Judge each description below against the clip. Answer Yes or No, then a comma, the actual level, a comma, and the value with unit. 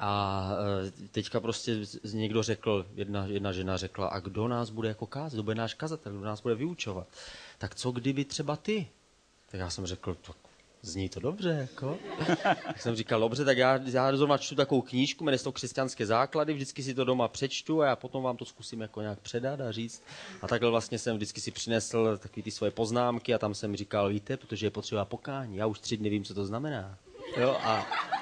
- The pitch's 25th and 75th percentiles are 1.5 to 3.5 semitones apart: No, average, 4.3 semitones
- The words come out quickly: Yes, fast, 210 wpm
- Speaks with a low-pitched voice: Yes, low, 115 Hz